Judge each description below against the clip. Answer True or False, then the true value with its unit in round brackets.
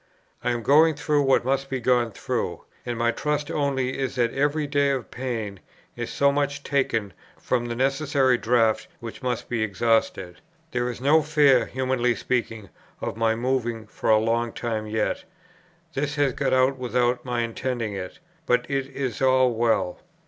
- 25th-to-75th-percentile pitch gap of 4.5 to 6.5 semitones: False (3.0 semitones)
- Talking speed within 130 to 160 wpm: False (170 wpm)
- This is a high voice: False (125 Hz)